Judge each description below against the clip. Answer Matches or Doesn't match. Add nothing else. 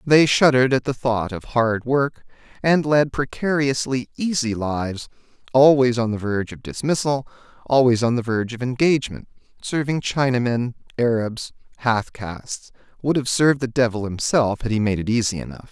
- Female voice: Doesn't match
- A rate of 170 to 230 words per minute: Doesn't match